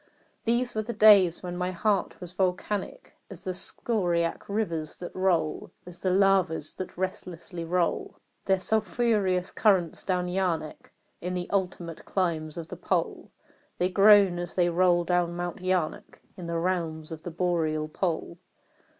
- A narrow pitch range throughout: Yes, narrow, 2.2 semitones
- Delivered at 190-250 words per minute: No, average, 150 wpm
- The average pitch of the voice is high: No, medium, 180 Hz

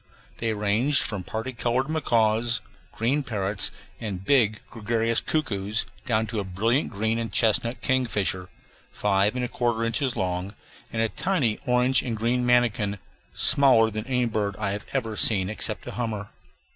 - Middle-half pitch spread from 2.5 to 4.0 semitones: Yes, average, 3.0 semitones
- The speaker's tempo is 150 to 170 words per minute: Yes, average, 160 wpm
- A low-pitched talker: Yes, low, 115 Hz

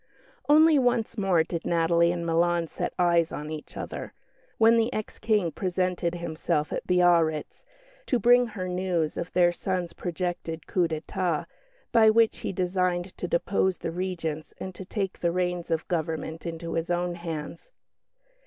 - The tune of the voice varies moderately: No, narrow, 2.3 semitones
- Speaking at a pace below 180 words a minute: Yes, average, 160 wpm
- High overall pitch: No, medium, 175 Hz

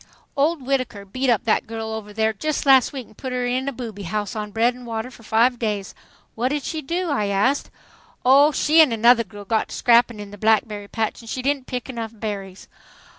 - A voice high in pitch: Yes, high, 230 Hz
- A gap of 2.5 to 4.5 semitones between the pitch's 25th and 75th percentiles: Yes, average, 3.5 semitones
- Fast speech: Yes, fast, 225 wpm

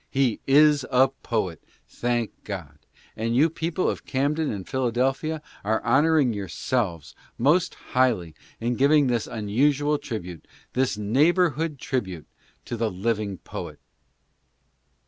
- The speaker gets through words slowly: Yes, slow, 120 wpm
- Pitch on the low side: Yes, low, 125 Hz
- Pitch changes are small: No, wide, 5.4 semitones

